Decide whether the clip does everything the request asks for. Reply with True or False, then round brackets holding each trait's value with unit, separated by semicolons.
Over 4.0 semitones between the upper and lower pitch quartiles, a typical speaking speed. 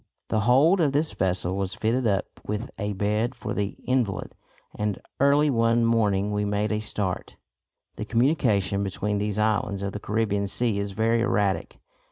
False (2.7 semitones; 170 wpm)